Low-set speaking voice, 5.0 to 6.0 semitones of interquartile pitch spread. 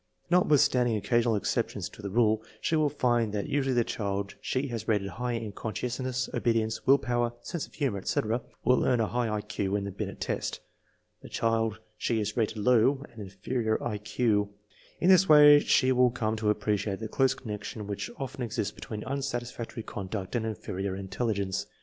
No: low, 115 Hz; average, 3.2 semitones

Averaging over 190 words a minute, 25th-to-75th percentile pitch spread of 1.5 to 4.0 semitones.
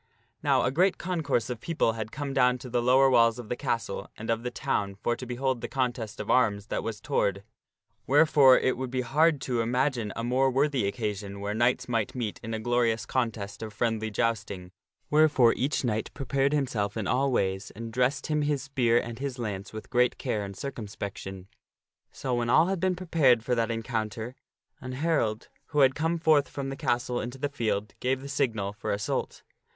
Yes: average, 200 wpm; average, 3.6 semitones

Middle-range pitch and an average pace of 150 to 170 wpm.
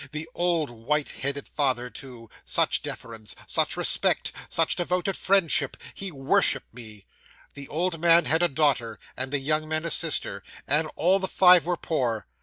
Yes: medium, 150 Hz; average, 165 wpm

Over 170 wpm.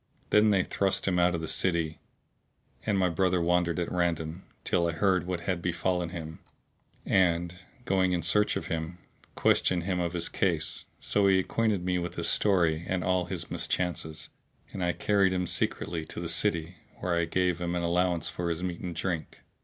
Yes: average, 190 wpm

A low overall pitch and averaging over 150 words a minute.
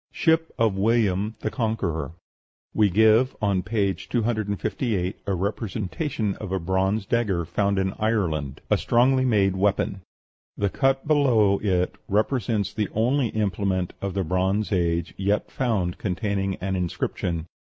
No: low, 100 Hz; slow, 135 wpm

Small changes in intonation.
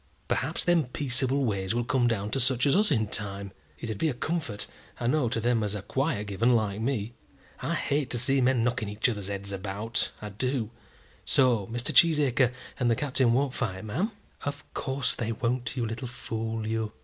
No: average, 3.7 semitones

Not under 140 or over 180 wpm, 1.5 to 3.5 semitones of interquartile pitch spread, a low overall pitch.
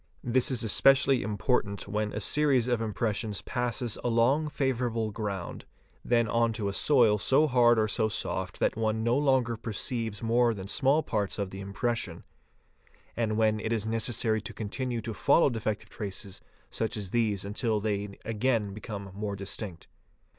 Yes: average, 165 wpm; average, 2.7 semitones; low, 110 Hz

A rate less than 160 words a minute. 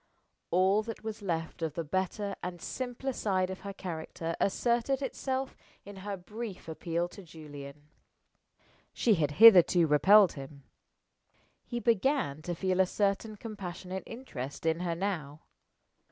Yes: average, 140 wpm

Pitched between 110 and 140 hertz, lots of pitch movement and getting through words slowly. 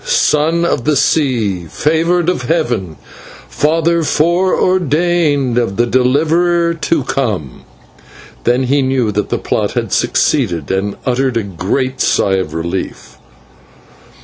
Yes: low, 135 Hz; wide, 7.4 semitones; slow, 130 wpm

